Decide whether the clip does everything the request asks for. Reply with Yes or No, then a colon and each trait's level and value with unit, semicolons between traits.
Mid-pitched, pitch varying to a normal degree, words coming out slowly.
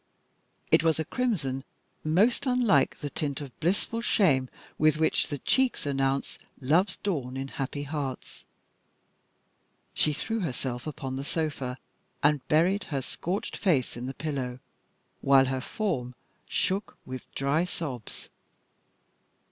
Yes: medium, 145 Hz; average, 4.7 semitones; slow, 130 wpm